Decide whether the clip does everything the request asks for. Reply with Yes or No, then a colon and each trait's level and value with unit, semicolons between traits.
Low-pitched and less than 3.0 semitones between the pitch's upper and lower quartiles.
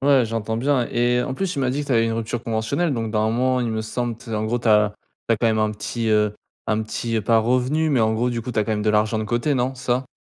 Yes: low, 115 Hz; narrow, 2.5 semitones